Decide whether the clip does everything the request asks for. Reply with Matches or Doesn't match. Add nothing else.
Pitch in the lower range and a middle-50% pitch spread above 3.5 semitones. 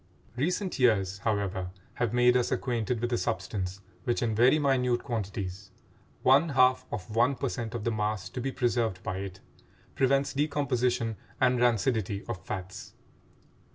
Matches